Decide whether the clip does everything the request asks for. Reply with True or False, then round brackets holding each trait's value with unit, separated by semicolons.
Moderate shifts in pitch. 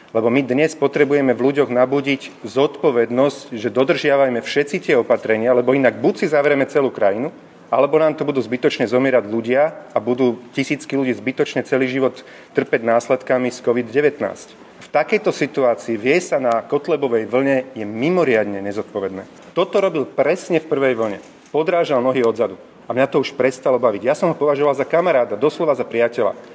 True (3.0 semitones)